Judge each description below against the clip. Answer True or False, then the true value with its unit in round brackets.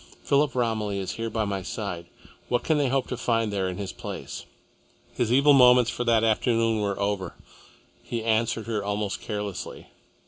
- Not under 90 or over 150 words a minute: False (175 wpm)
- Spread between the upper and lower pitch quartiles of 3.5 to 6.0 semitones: False (3.1 semitones)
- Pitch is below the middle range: True (110 Hz)